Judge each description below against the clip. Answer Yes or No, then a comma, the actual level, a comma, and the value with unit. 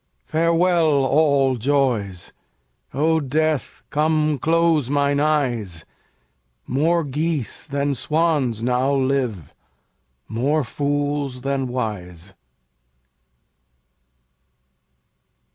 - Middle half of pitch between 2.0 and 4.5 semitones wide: Yes, average, 3.5 semitones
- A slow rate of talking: Yes, slow, 75 wpm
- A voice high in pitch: No, medium, 140 Hz